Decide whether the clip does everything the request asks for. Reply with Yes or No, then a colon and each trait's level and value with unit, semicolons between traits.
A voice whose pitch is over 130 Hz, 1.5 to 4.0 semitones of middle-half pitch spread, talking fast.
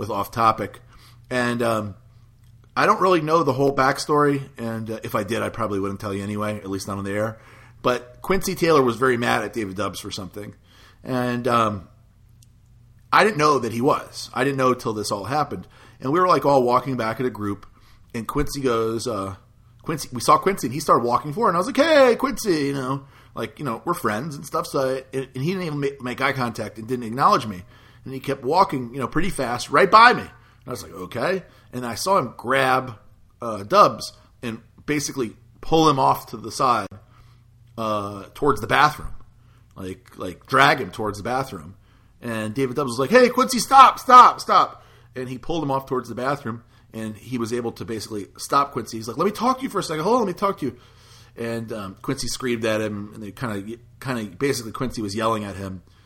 No: low, 120 Hz; average, 3.7 semitones; fast, 225 wpm